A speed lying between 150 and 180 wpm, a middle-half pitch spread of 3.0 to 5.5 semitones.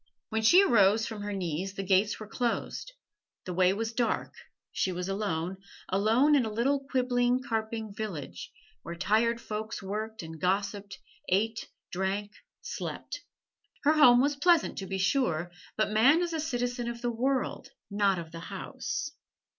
Yes: average, 160 wpm; average, 4.2 semitones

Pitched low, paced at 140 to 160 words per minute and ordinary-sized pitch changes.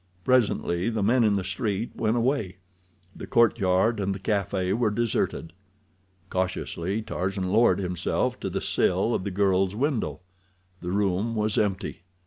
Yes: low, 100 Hz; average, 145 wpm; average, 3.3 semitones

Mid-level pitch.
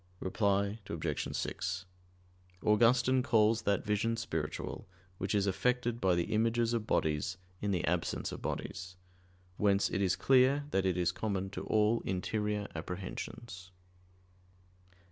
No: low, 105 Hz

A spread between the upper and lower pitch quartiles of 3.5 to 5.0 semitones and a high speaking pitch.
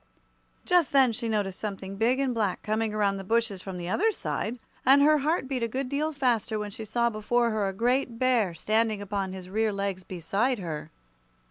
Yes: average, 4.3 semitones; high, 220 Hz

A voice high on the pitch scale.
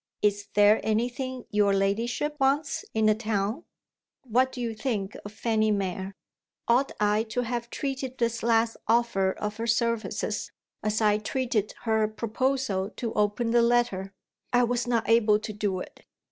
Yes: high, 225 Hz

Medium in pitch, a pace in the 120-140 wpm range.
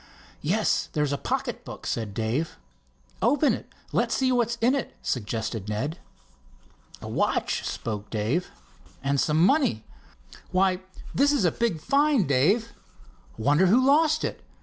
Yes: medium, 175 Hz; slow, 135 wpm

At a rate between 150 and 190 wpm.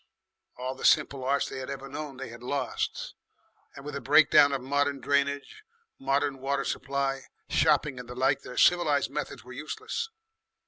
Yes: average, 170 wpm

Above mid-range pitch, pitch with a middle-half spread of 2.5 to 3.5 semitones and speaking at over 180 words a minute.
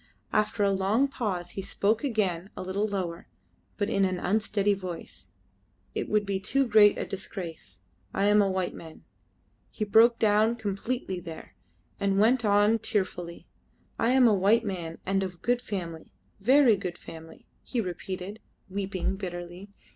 No: high, 200 Hz; average, 2.9 semitones; average, 155 wpm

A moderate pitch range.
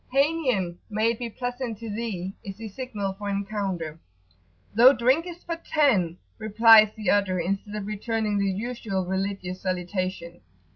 Yes: average, 3.6 semitones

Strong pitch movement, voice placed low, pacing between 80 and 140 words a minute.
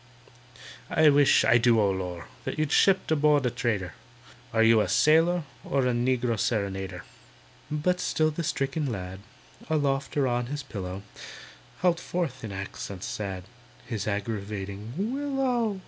Yes: wide, 7.2 semitones; low, 125 Hz; slow, 135 wpm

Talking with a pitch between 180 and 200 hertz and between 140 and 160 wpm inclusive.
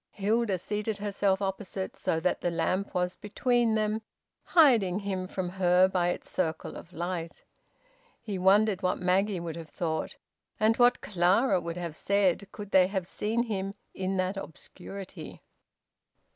Yes: high, 190 Hz; average, 150 wpm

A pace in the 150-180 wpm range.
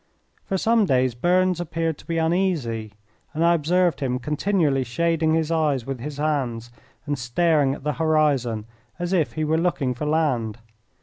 Yes: average, 170 wpm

